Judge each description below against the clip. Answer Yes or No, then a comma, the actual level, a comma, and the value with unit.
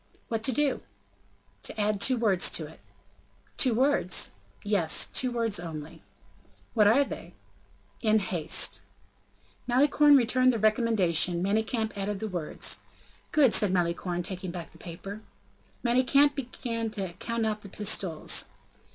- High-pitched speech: Yes, high, 215 Hz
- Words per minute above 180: No, slow, 135 wpm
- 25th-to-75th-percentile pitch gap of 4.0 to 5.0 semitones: Yes, average, 4.7 semitones